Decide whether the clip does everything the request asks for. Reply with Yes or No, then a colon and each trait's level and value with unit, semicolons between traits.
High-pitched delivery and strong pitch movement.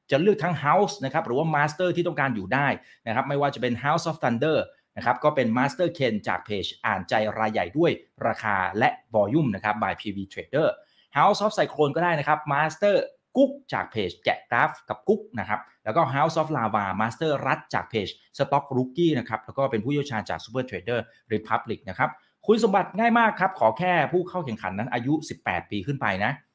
No: medium, 140 Hz; wide, 7.4 semitones